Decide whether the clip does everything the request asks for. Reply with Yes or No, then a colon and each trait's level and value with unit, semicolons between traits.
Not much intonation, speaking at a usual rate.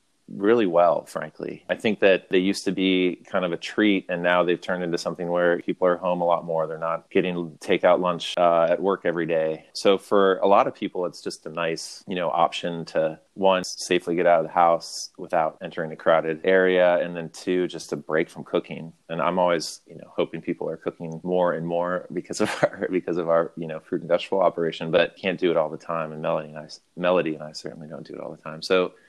No: narrow, 1.8 semitones; fast, 245 wpm